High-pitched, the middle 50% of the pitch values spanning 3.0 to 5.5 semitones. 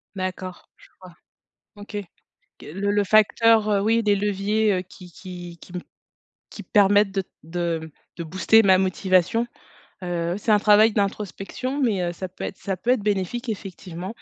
No: high, 195 Hz; narrow, 2.5 semitones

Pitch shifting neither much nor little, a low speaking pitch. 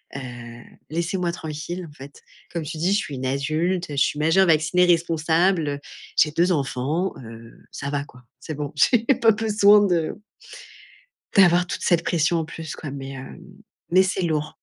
No: average, 3.7 semitones; medium, 160 Hz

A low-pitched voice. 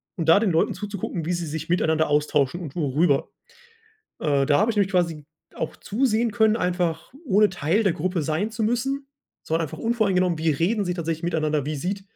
No: medium, 175 Hz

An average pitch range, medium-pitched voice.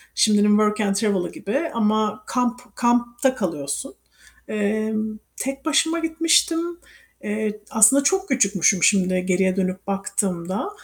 No: average, 4.3 semitones; high, 215 Hz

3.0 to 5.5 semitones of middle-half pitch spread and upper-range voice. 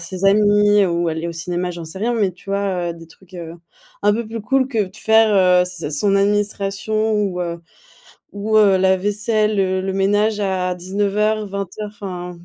No: narrow, 2.6 semitones; high, 195 Hz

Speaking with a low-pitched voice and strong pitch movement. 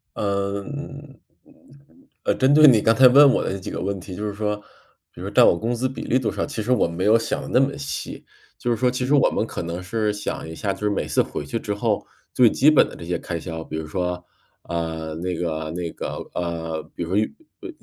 Yes: low, 105 Hz; wide, 6.5 semitones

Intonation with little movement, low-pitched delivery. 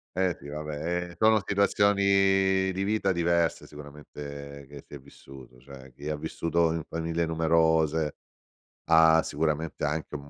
No: average, 3.2 semitones; very low, 80 Hz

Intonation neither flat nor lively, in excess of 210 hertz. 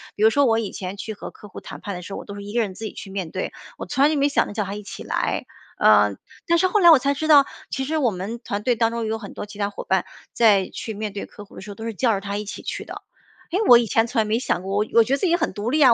Yes: average, 3.9 semitones; high, 220 Hz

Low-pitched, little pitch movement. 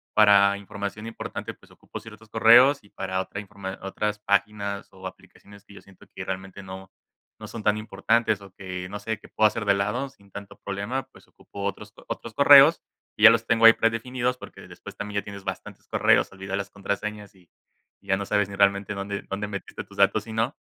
Yes: low, 100 Hz; narrow, 2.1 semitones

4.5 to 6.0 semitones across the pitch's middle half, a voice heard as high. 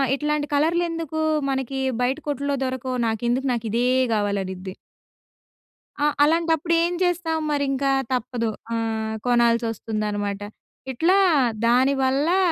Yes: average, 4.8 semitones; very high, 265 Hz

